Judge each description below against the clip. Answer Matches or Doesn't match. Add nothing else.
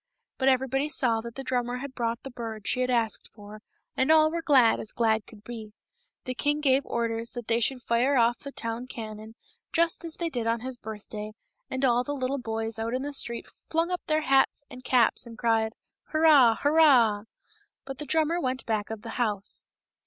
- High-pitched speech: Matches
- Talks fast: Matches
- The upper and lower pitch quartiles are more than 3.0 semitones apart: Matches